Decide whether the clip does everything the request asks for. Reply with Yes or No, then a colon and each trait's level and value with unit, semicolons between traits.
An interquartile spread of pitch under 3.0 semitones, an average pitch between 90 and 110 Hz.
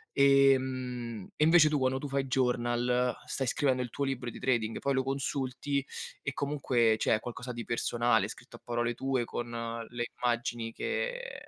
No: narrow, 2.4 semitones; low, 125 Hz